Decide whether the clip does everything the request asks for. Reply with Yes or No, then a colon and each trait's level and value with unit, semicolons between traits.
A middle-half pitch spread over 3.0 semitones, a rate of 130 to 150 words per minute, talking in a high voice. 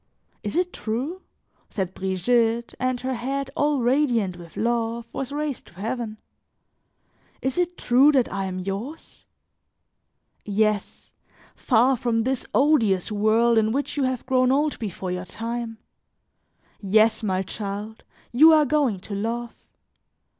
Yes: average, 3.9 semitones; slow, 135 wpm; high, 235 Hz